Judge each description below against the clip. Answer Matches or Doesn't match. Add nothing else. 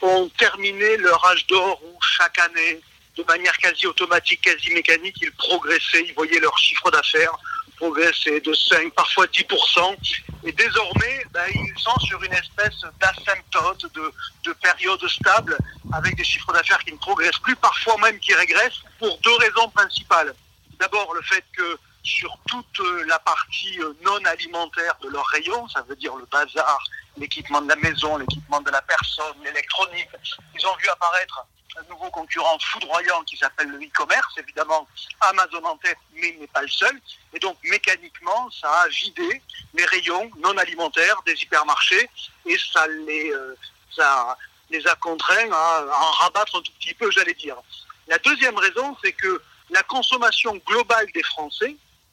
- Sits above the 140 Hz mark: Matches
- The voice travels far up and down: Matches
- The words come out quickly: Doesn't match